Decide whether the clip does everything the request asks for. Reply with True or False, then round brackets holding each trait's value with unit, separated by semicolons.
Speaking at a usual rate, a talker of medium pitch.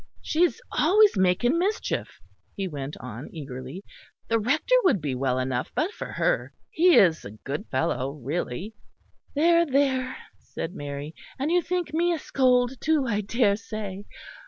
False (155 wpm; 215 Hz)